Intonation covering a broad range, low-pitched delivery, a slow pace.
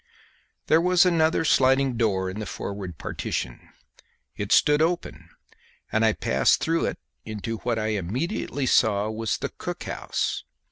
No: wide, 6.9 semitones; low, 115 Hz; average, 145 wpm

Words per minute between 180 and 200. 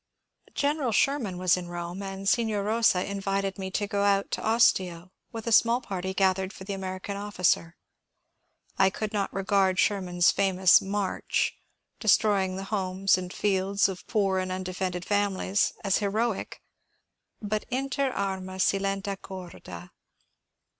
No: average, 155 wpm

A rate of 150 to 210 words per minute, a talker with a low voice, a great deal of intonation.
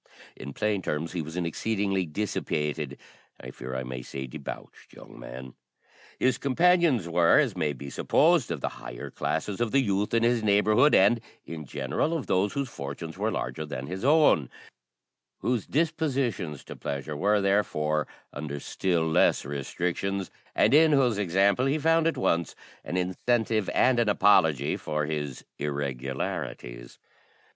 Yes: average, 155 wpm; very low, 90 Hz; wide, 8.2 semitones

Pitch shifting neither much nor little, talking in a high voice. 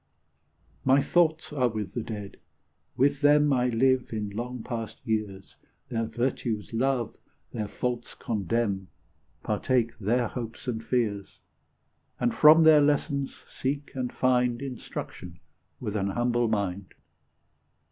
No: average, 3.4 semitones; low, 120 Hz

